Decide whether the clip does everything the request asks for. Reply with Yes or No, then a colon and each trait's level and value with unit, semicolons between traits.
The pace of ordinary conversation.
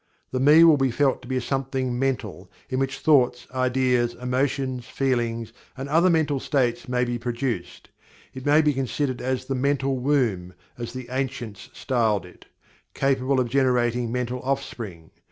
Yes: average, 160 wpm